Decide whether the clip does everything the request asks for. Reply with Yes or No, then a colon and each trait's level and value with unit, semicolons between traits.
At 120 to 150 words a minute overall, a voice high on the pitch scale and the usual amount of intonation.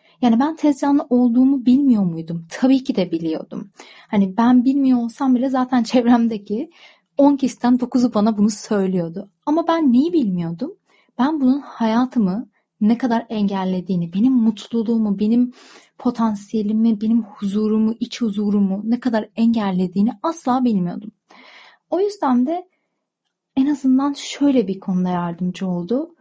Yes: average, 130 wpm; high, 235 Hz; average, 4.1 semitones